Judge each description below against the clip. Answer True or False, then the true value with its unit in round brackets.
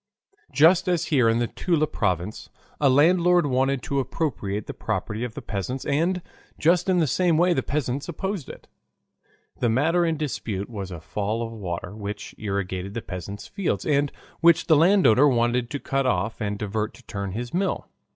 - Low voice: True (130 Hz)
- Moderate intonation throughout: False (7.3 semitones)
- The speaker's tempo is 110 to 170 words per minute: False (180 wpm)